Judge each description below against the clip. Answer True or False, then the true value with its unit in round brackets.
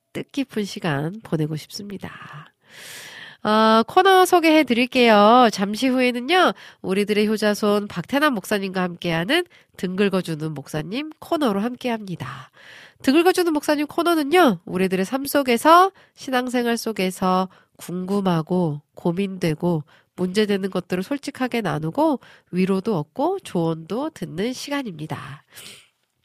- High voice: True (210 Hz)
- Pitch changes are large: True (6.9 semitones)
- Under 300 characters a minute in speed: True (290 characters per minute)